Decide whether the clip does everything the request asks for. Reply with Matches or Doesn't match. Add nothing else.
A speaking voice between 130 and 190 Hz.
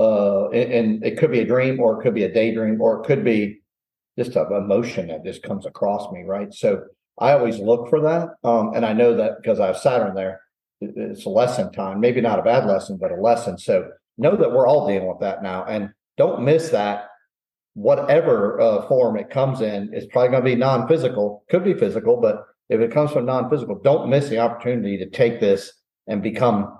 Doesn't match